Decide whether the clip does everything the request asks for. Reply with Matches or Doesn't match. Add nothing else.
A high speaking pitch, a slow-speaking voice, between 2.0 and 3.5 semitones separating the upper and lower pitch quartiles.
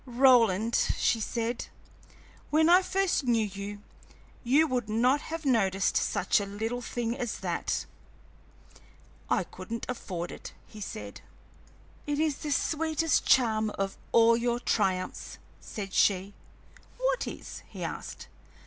Doesn't match